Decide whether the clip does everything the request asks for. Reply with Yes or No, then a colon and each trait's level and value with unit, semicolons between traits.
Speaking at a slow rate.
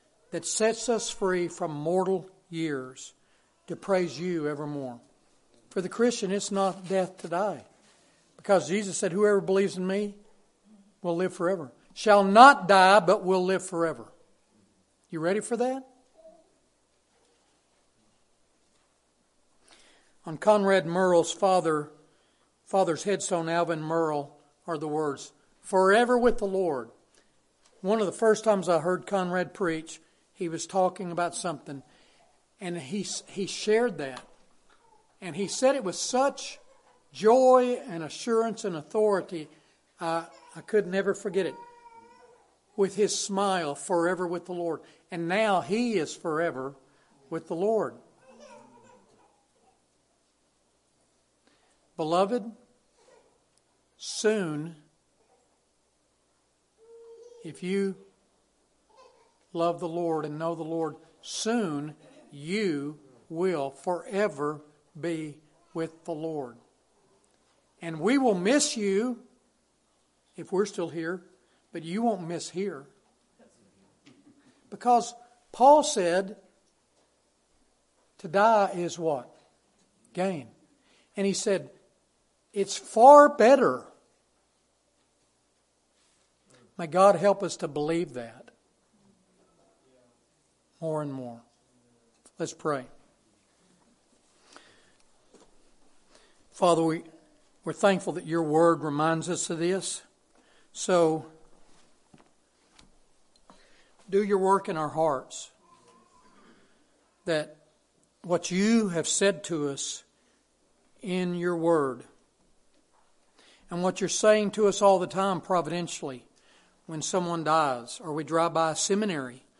Yes: slow, 105 wpm